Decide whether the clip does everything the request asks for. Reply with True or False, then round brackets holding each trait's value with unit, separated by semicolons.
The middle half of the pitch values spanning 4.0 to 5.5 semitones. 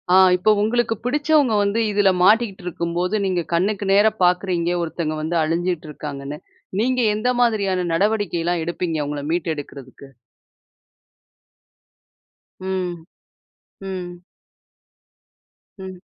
False (3.5 semitones)